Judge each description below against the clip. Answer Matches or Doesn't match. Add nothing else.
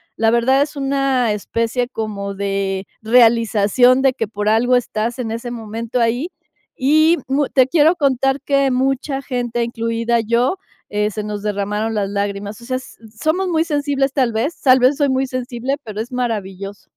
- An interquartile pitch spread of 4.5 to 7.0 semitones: Doesn't match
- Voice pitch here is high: Matches